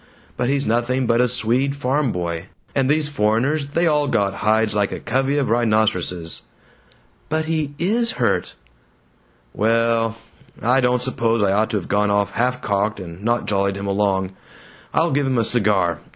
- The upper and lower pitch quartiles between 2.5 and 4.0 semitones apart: No, average, 4.8 semitones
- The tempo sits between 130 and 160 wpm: No, average, 175 wpm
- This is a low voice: Yes, low, 115 Hz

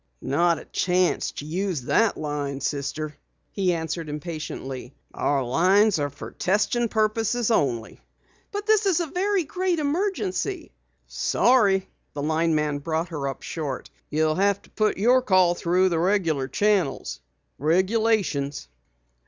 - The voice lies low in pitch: No, medium, 180 Hz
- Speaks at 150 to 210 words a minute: No, slow, 135 wpm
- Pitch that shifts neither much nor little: No, wide, 6.8 semitones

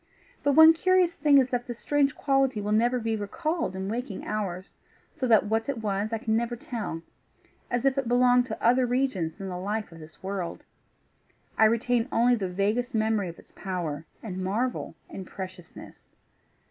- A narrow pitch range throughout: No, average, 4.3 semitones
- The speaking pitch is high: Yes, high, 225 Hz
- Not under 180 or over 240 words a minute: Yes, average, 185 wpm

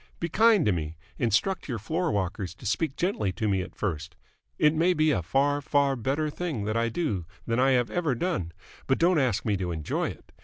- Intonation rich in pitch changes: Yes, wide, 8.1 semitones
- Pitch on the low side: Yes, low, 130 Hz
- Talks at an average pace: No, fast, 220 wpm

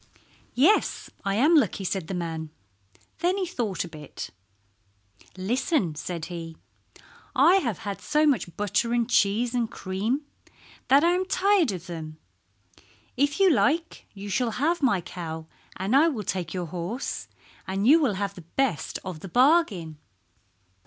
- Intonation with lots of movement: Yes, wide, 8.2 semitones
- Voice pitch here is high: Yes, high, 210 Hz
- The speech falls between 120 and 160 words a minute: Yes, average, 155 wpm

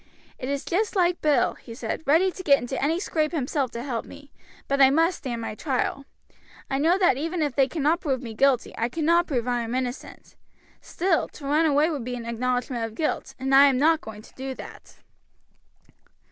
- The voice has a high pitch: Yes, very high, 275 Hz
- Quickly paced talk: Yes, fast, 210 wpm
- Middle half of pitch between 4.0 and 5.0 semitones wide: Yes, average, 4.3 semitones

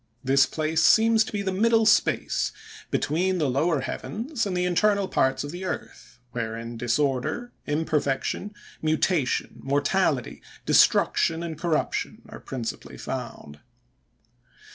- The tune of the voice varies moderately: No, wide, 6.1 semitones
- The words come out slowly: Yes, slow, 120 wpm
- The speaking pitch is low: No, medium, 160 Hz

